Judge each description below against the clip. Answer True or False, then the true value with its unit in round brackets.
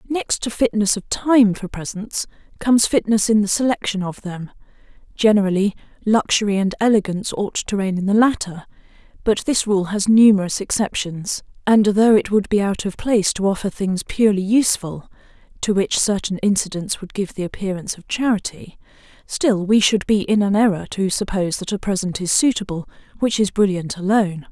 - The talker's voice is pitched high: True (200 Hz)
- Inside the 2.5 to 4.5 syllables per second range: False (4.8 syllables/s)